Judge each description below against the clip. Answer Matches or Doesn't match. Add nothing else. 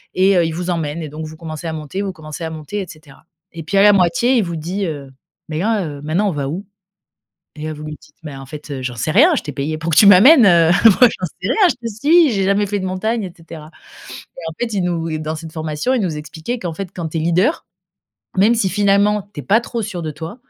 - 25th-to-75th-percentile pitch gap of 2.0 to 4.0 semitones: Doesn't match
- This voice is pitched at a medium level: Matches